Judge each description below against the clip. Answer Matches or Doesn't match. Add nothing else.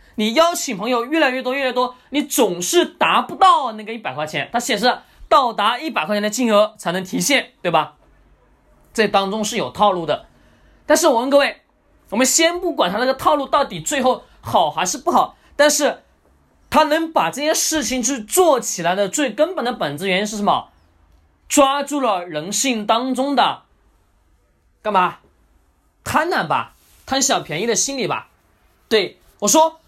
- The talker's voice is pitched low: Doesn't match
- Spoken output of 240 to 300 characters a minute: Matches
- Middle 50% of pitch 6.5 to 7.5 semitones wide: Doesn't match